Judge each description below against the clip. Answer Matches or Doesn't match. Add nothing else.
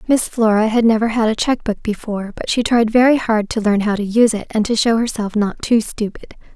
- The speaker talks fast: Matches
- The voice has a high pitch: Matches